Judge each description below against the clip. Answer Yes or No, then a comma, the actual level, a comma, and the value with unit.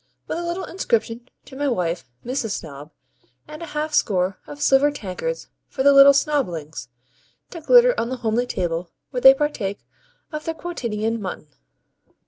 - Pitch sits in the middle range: No, very high, 255 Hz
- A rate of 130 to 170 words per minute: Yes, average, 160 wpm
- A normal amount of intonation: No, wide, 7.3 semitones